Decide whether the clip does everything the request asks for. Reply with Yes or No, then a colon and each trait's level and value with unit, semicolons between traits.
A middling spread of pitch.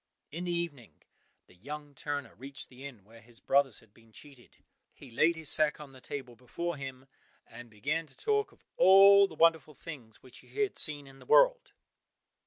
Yes: average, 4.7 semitones